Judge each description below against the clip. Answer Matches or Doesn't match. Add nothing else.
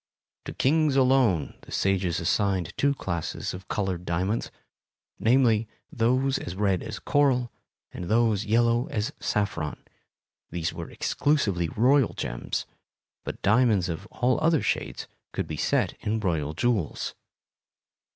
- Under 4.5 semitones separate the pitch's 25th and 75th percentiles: Doesn't match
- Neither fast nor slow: Doesn't match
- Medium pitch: Doesn't match